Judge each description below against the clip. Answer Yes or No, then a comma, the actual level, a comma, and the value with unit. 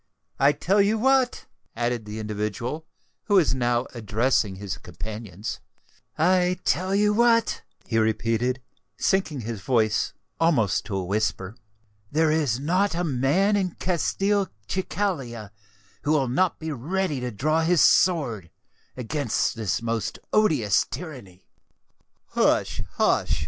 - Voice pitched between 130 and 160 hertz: Yes, low, 135 Hz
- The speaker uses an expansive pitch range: Yes, wide, 8.5 semitones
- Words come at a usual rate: No, slow, 125 wpm